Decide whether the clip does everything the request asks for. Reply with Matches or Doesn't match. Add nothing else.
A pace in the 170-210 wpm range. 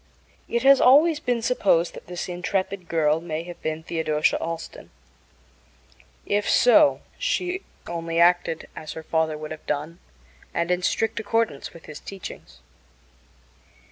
Doesn't match